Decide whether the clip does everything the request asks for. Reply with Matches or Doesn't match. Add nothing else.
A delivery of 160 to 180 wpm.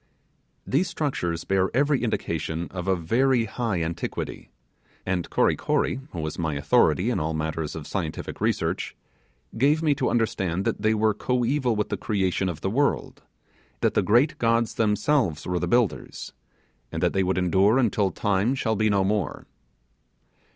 Matches